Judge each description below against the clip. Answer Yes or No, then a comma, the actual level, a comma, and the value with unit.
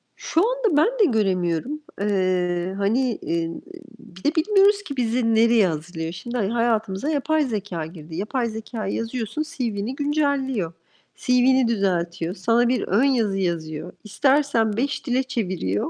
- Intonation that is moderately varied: No, wide, 6.3 semitones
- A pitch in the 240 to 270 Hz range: No, high, 225 Hz